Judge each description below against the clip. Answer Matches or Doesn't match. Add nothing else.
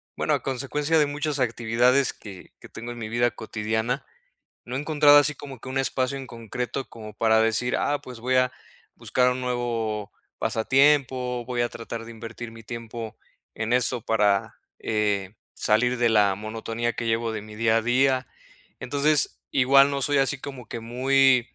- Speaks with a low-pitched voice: Matches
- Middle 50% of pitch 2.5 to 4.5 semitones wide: Matches